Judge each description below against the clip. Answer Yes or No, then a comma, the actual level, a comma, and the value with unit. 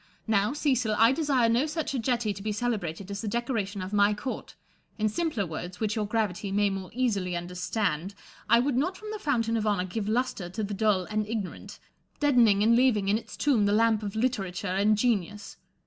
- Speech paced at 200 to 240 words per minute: Yes, fast, 205 wpm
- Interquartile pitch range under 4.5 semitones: Yes, average, 3.2 semitones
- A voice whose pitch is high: Yes, high, 215 Hz